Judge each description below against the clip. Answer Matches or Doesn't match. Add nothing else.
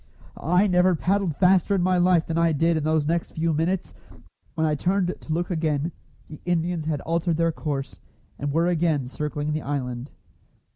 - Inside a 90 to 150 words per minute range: Doesn't match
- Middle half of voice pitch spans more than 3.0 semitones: Doesn't match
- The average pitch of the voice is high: Doesn't match